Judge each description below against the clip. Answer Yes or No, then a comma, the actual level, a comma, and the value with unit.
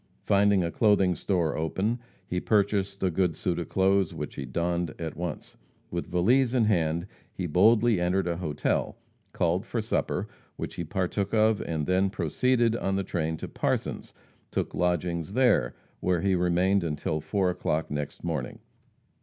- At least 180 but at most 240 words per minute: No, average, 160 wpm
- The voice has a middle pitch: No, very low, 90 Hz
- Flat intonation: No, average, 3.0 semitones